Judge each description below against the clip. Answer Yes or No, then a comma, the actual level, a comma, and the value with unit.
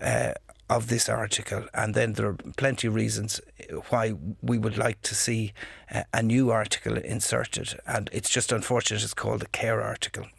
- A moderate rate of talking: Yes, average, 175 wpm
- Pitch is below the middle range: Yes, low, 110 Hz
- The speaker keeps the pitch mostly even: Yes, narrow, 1.8 semitones